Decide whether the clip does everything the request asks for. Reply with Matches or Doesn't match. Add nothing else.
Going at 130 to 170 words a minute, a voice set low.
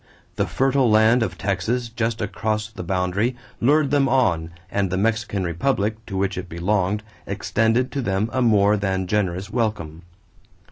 Matches